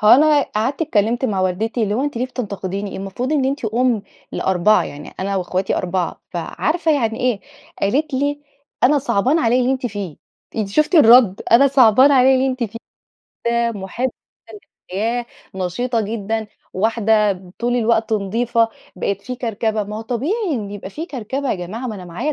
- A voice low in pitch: No, high, 230 Hz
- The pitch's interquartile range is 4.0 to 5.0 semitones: Yes, average, 4.4 semitones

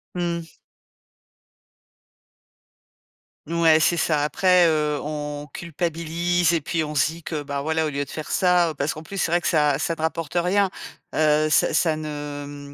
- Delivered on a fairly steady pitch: Yes, narrow, 2.3 semitones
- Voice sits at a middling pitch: Yes, medium, 155 Hz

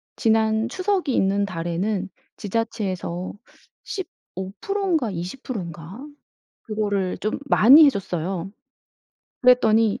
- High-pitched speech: Yes, high, 210 Hz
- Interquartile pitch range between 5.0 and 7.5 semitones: No, average, 4.2 semitones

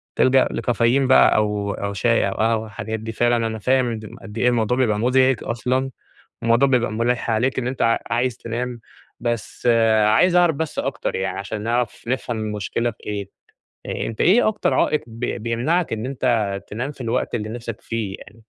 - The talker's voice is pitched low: Yes, low, 115 Hz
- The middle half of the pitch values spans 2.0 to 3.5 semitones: Yes, average, 2.7 semitones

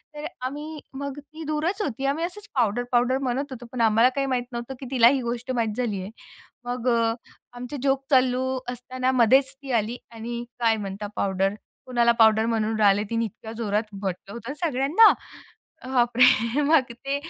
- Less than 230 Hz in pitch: No, high, 245 Hz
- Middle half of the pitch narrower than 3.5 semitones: Yes, average, 3.0 semitones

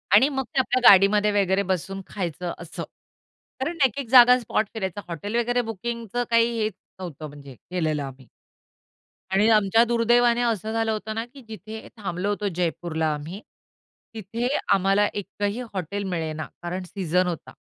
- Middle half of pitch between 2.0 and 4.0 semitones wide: No, average, 4.5 semitones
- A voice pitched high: Yes, high, 205 Hz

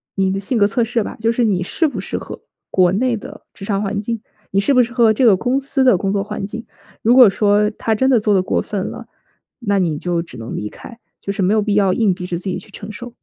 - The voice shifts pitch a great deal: No, average, 3.2 semitones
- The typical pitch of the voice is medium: No, high, 210 Hz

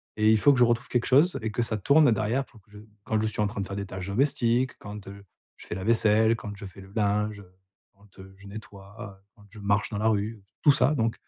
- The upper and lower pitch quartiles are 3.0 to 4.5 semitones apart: No, narrow, 2.5 semitones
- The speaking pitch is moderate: No, low, 105 Hz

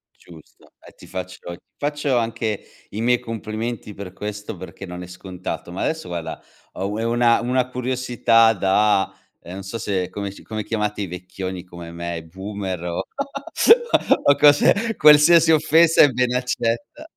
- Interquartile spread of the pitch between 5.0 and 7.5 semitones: Yes, average, 5.3 semitones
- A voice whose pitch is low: Yes, low, 105 Hz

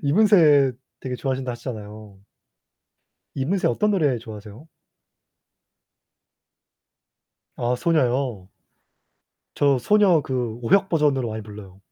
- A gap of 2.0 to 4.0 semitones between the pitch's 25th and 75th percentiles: No, wide, 5.6 semitones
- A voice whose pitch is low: Yes, low, 130 Hz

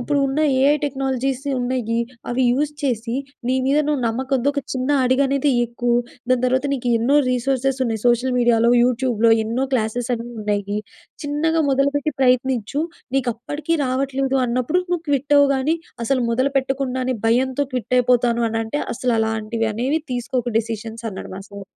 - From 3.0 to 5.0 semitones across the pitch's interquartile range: No, narrow, 2.6 semitones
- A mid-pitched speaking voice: No, very high, 255 Hz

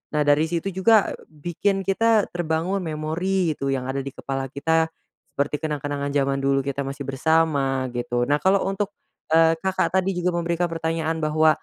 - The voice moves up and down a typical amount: Yes, average, 3.9 semitones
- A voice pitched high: No, medium, 160 Hz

